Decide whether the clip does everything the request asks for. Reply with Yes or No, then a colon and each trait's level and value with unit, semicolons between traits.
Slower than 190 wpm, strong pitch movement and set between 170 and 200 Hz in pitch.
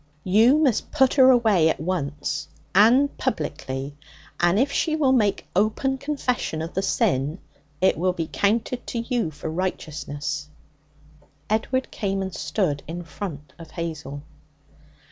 Yes: average, 140 wpm; wide, 7.5 semitones; high, 190 Hz